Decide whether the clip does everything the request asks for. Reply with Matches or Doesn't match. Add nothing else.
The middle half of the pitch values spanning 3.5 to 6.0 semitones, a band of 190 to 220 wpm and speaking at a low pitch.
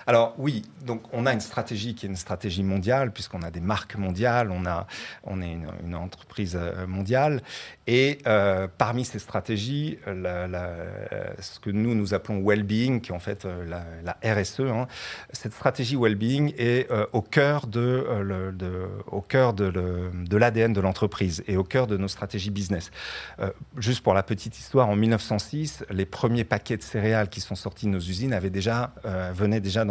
Matches